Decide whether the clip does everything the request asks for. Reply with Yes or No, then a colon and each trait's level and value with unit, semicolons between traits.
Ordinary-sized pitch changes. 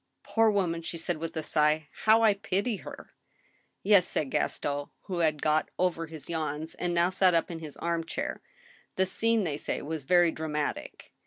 Yes: average, 3.3 semitones